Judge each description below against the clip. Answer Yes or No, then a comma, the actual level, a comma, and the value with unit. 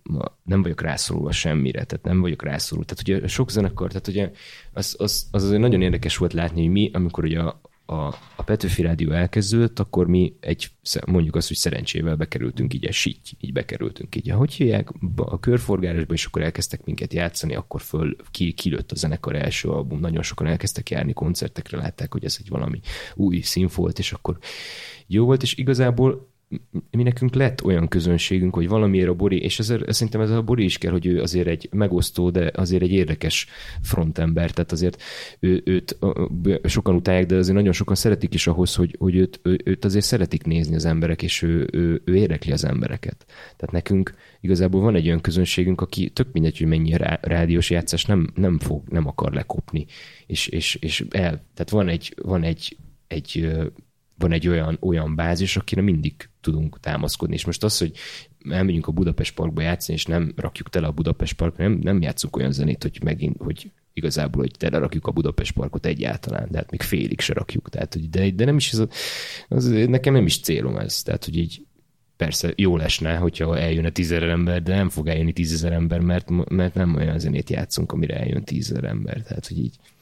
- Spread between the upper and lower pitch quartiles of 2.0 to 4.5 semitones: Yes, average, 3.3 semitones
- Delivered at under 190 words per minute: No, average, 195 wpm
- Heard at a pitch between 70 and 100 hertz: Yes, very low, 90 Hz